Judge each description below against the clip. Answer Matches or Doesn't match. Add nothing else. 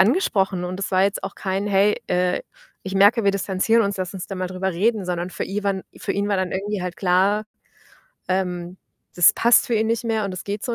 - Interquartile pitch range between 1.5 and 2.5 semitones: Matches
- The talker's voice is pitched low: Doesn't match